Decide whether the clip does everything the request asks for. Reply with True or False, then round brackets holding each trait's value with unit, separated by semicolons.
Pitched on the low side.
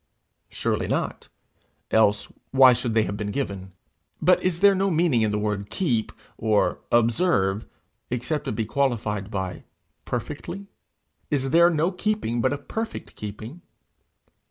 True (120 Hz)